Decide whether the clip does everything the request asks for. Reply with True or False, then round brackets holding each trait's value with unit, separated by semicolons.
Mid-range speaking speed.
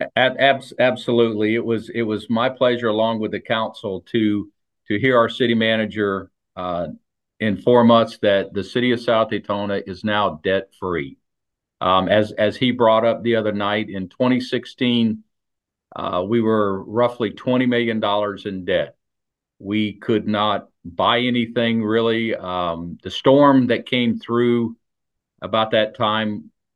True (145 wpm)